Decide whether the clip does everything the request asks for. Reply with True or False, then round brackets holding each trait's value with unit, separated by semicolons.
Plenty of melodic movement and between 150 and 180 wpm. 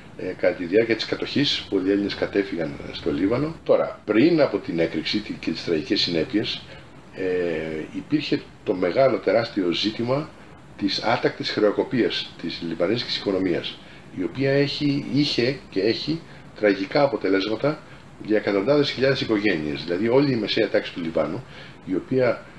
False (6.7 semitones; 140 wpm)